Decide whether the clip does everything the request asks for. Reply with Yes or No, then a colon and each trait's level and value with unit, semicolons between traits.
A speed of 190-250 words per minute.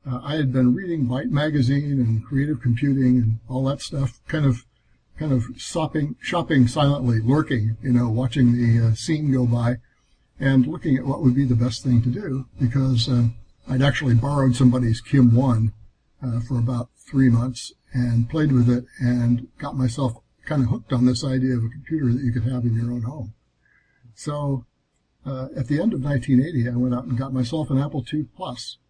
Yes: average, 195 wpm